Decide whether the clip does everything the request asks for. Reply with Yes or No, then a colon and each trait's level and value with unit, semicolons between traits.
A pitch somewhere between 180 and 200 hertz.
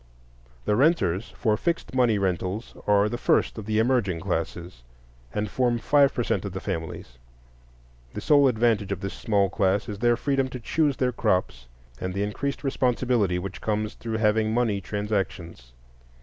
No: low, 105 Hz